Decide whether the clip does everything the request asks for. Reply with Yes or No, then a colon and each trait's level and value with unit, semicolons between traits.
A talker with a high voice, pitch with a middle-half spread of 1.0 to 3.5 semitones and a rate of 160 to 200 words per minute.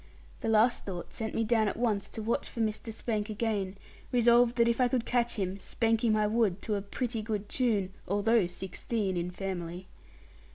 Yes: high, 220 Hz; average, 2.9 semitones; average, 195 wpm